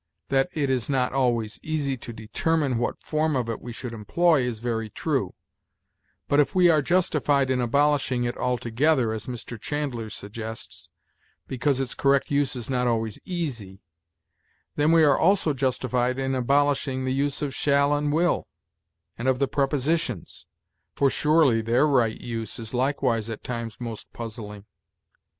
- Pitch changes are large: No, average, 3.7 semitones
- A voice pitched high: No, low, 130 Hz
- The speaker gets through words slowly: No, average, 160 wpm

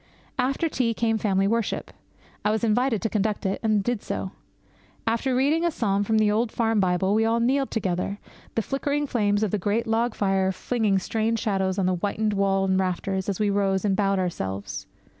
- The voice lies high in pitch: Yes, high, 210 Hz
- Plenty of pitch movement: No, average, 3.0 semitones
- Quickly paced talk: No, average, 195 wpm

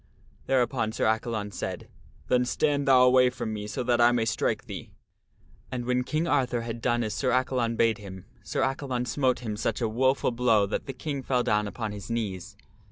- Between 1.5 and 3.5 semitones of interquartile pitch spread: Yes, narrow, 2.6 semitones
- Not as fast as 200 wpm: No, fast, 205 wpm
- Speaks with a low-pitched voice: Yes, low, 120 Hz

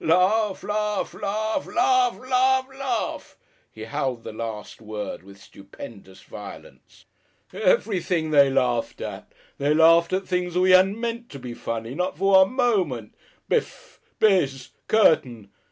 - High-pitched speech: No, medium, 180 Hz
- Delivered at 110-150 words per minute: Yes, slow, 135 wpm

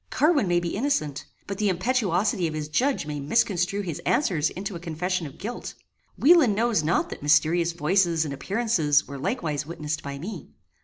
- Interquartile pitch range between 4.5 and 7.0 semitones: Yes, average, 5.3 semitones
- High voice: No, medium, 175 Hz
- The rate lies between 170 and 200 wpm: Yes, average, 175 wpm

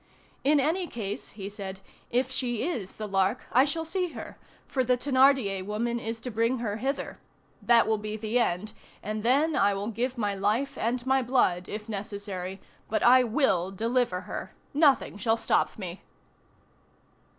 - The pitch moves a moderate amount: Yes, average, 4.2 semitones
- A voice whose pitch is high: Yes, high, 230 Hz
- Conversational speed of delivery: Yes, average, 170 wpm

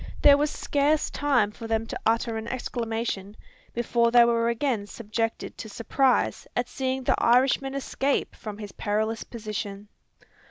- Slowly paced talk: No, average, 150 wpm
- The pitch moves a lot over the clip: No, average, 3.1 semitones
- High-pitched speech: Yes, high, 235 Hz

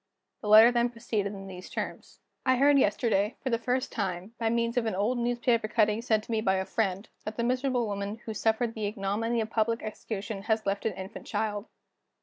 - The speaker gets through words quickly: Yes, fast, 210 wpm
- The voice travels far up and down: No, narrow, 2.6 semitones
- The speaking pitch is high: Yes, high, 220 Hz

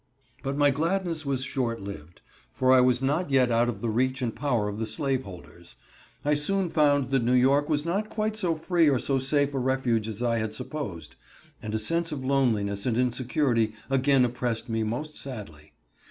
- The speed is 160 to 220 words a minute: Yes, average, 195 wpm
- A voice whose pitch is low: Yes, low, 130 Hz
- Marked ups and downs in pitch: No, average, 4.2 semitones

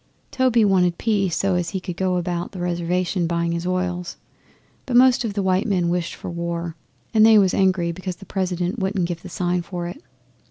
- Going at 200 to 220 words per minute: Yes, fast, 205 wpm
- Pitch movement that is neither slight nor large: No, narrow, 2.0 semitones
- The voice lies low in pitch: No, medium, 180 Hz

